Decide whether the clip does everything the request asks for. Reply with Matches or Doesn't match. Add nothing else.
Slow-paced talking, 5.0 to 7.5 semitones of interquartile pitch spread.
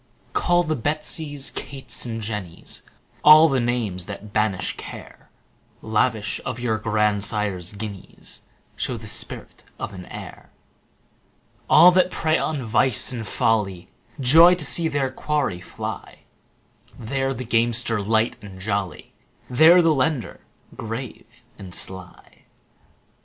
Matches